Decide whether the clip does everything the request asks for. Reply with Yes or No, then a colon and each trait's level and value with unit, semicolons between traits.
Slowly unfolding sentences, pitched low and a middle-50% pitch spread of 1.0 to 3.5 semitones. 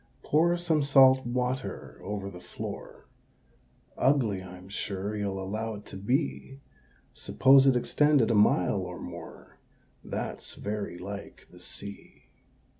No: slow, 125 wpm; low, 110 Hz; average, 5.3 semitones